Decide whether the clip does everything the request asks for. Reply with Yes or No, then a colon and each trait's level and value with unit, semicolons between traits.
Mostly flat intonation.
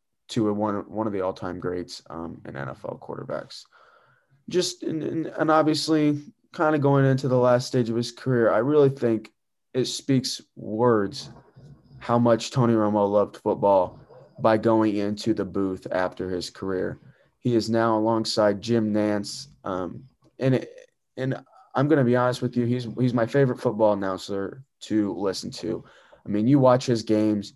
No: average, 3.9 semitones